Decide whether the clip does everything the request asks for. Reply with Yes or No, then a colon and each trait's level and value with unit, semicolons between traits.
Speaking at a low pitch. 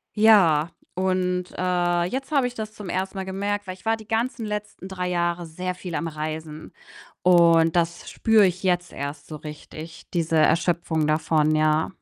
No: medium, 175 Hz